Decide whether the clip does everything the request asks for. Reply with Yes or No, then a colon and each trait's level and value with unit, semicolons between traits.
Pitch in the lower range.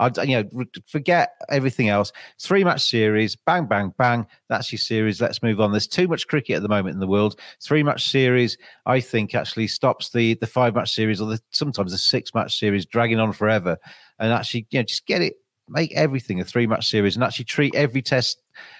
Yes: low, 115 Hz